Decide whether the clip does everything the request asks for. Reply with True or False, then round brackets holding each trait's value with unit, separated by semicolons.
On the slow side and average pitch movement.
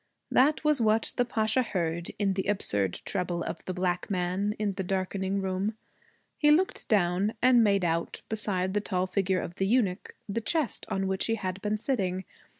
False (185 wpm; 3.0 semitones)